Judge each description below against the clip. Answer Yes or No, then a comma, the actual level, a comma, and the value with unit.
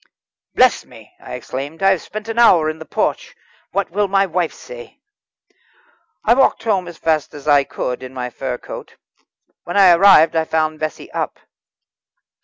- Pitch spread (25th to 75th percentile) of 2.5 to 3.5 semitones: No, average, 4.3 semitones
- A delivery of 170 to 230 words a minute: Yes, average, 175 wpm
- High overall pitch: No, medium, 165 Hz